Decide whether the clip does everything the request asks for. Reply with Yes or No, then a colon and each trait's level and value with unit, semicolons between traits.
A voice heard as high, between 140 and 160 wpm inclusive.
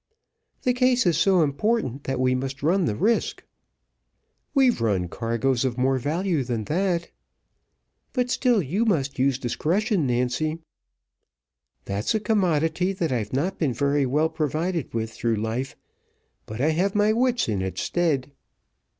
No: medium, 150 Hz; average, 150 wpm